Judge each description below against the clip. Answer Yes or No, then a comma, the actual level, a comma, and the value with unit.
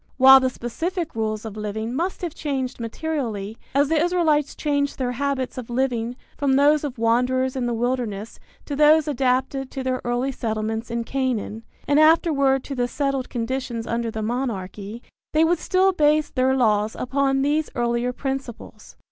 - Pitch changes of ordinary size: Yes, average, 3.5 semitones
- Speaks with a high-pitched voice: Yes, very high, 260 Hz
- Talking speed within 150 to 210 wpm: Yes, average, 165 wpm